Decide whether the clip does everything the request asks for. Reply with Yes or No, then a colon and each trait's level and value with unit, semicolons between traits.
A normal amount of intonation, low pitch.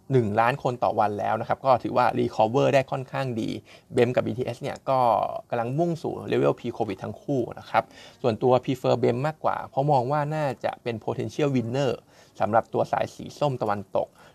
Yes: average, 3.4 semitones; low, 130 Hz